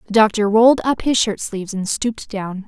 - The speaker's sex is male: No, female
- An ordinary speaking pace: No, fast, 225 wpm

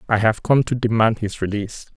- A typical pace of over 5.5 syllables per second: Yes, 5.9 syllables/s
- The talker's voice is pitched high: No, low, 110 Hz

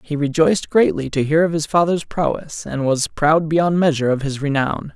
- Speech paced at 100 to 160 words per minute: No, fast, 205 wpm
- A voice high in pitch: No, medium, 155 Hz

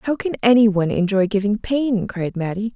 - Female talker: Yes, female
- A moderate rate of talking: Yes, average, 195 wpm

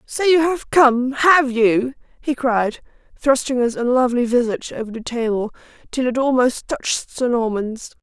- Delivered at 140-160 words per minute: Yes, average, 155 wpm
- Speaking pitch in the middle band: No, very high, 250 Hz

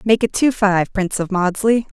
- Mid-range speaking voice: No, high, 205 Hz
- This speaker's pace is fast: Yes, fast, 210 wpm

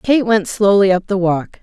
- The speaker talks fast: Yes, fast, 220 wpm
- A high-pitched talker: Yes, high, 195 Hz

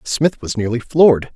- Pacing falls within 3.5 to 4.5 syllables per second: No, 4.8 syllables/s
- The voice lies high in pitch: No, low, 130 Hz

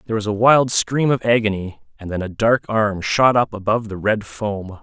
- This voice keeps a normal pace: No, fast, 225 wpm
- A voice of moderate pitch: No, low, 110 Hz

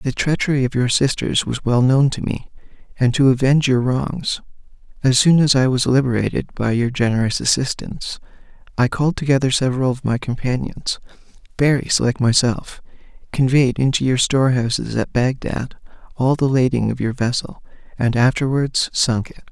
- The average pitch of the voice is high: No, low, 130 Hz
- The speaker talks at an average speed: Yes, average, 155 wpm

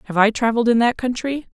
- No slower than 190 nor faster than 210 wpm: No, fast, 230 wpm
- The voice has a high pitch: Yes, high, 235 Hz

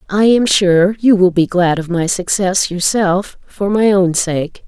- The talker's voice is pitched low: No, high, 190 Hz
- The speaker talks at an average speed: Yes, average, 195 wpm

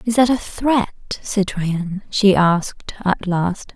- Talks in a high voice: Yes, high, 200 Hz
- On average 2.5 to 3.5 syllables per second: Yes, 3.2 syllables/s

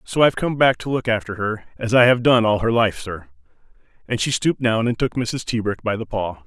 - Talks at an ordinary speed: No, fast, 250 wpm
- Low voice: Yes, low, 115 Hz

